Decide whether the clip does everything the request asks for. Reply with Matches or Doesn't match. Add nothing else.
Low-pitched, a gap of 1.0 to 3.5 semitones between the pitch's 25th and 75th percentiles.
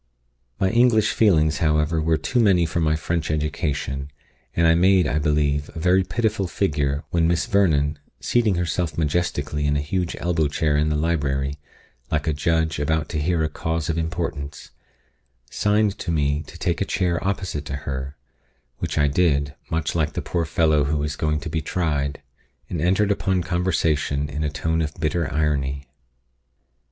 Matches